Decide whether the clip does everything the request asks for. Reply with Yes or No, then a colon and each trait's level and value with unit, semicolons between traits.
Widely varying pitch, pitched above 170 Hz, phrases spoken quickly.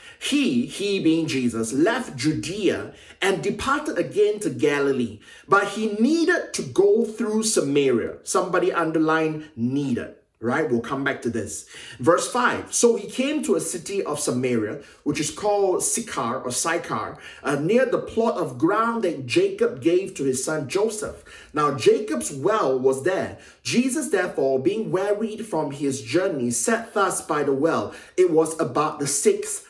No: wide, 8.8 semitones; medium, 185 Hz; average, 160 wpm